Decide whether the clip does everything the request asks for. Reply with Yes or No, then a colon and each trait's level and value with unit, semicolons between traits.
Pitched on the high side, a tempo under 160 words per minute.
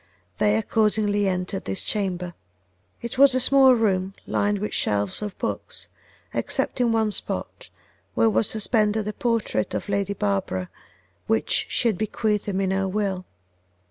Yes: high, 205 Hz; average, 150 wpm